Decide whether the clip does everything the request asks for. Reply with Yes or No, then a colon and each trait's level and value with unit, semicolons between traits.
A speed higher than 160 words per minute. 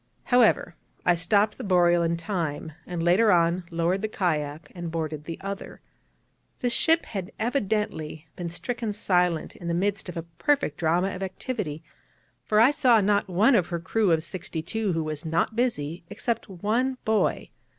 Yes: average, 170 wpm